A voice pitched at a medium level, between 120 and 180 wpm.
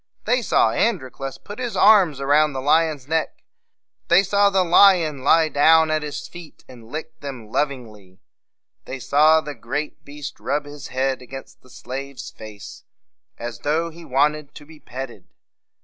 Yes: medium, 145 Hz; average, 165 wpm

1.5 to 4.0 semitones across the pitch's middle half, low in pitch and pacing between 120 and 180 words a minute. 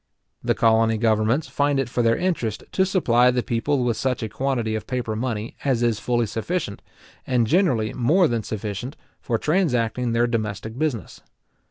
Yes: average, 3.2 semitones; low, 120 Hz; average, 170 wpm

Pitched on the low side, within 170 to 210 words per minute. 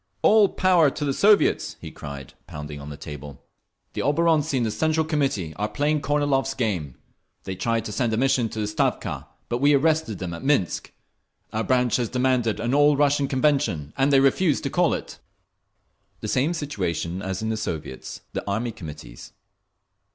Yes: low, 125 Hz; average, 180 wpm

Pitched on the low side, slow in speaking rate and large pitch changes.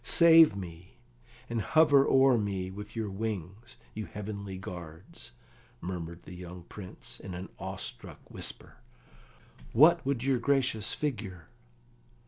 Yes: low, 100 Hz; slow, 120 wpm; wide, 5.9 semitones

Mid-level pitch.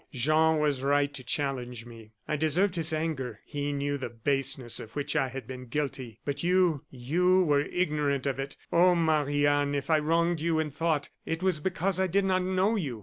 Yes: medium, 145 Hz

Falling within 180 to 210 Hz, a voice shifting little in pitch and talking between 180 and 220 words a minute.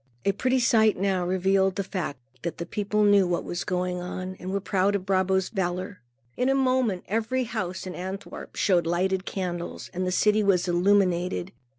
Yes: high, 190 Hz; narrow, 2.1 semitones; average, 190 wpm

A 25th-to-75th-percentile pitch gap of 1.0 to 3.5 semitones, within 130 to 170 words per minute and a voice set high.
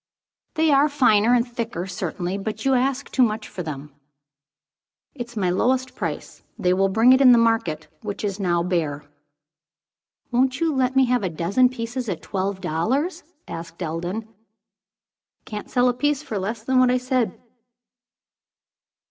No: wide, 5.5 semitones; average, 160 wpm; high, 225 Hz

